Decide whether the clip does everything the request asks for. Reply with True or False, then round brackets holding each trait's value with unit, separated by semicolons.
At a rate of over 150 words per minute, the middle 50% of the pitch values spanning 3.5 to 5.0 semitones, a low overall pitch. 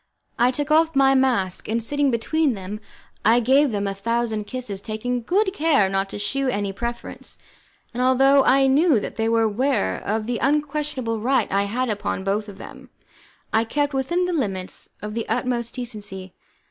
False (180 wpm; 4.5 semitones; 240 Hz)